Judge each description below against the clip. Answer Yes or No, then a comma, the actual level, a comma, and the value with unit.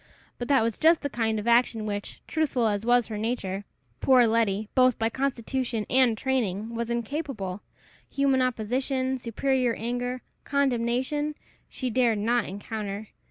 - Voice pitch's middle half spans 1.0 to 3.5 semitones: Yes, average, 3.0 semitones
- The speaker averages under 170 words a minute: Yes, average, 150 wpm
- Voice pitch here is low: No, high, 240 Hz